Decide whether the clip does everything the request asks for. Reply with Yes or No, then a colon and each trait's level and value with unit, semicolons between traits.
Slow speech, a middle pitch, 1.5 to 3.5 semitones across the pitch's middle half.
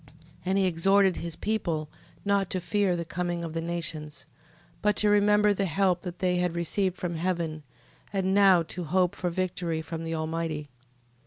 No: average, 180 wpm; medium, 180 Hz; average, 2.8 semitones